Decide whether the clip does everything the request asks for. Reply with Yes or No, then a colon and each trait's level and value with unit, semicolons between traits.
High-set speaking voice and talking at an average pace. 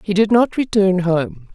Yes: high, 195 Hz; average, 195 wpm